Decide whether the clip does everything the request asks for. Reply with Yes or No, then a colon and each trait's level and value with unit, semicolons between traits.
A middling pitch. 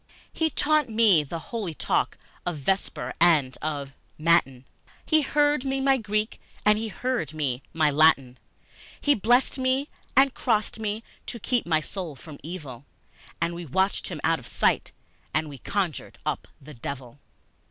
Yes: medium, 175 Hz